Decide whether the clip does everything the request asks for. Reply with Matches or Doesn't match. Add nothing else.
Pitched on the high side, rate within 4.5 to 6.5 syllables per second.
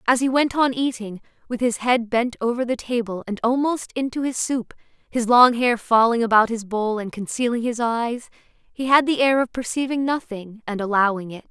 Matches